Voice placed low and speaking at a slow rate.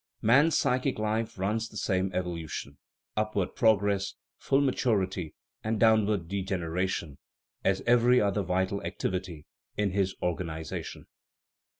Yes: low, 100 Hz; slow, 110 wpm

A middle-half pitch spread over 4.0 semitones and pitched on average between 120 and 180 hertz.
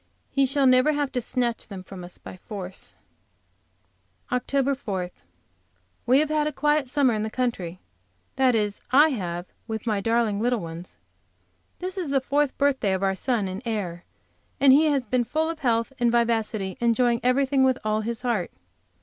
No: average, 4.7 semitones; high, 240 Hz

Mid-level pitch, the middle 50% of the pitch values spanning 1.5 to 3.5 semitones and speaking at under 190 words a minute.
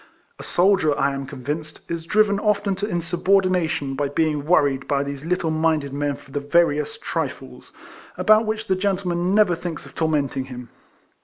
No: medium, 160 Hz; average, 4.6 semitones; average, 170 wpm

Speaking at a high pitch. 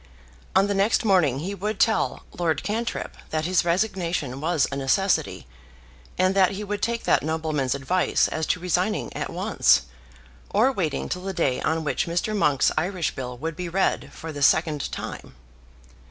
No: medium, 175 Hz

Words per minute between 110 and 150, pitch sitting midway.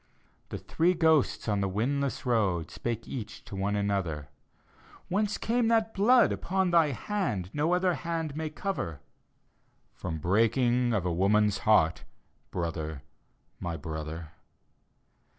No: slow, 135 wpm; low, 115 Hz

